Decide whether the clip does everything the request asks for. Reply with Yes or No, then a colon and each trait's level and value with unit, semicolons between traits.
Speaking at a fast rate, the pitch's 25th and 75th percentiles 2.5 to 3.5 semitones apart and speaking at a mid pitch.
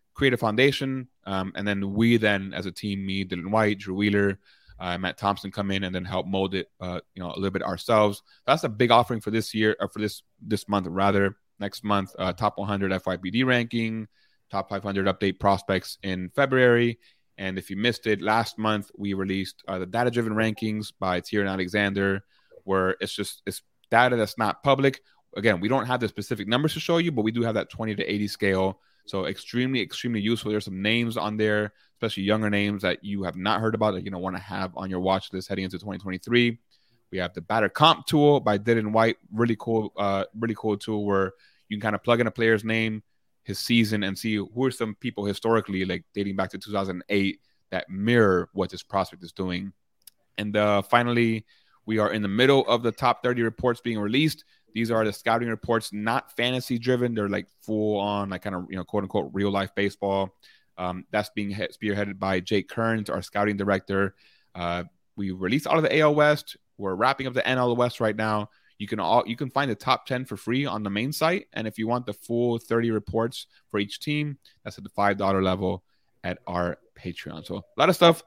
No: fast, 215 wpm; average, 3.0 semitones; low, 105 Hz